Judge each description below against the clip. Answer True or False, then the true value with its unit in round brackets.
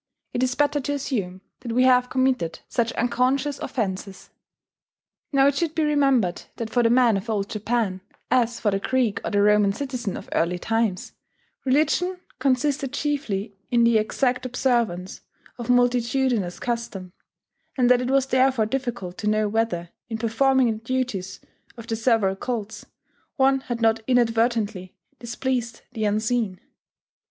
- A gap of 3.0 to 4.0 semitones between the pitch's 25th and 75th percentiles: True (3.4 semitones)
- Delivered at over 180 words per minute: False (150 wpm)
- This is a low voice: False (235 Hz)